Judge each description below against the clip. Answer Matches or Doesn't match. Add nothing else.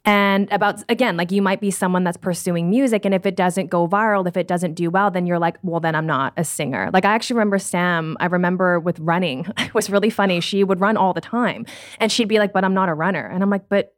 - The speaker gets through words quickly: Matches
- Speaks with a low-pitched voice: Doesn't match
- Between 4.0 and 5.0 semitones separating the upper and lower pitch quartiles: Doesn't match